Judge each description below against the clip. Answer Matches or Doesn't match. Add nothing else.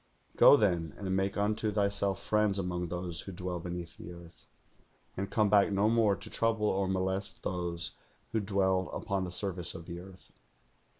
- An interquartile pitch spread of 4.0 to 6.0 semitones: Doesn't match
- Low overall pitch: Matches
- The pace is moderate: Matches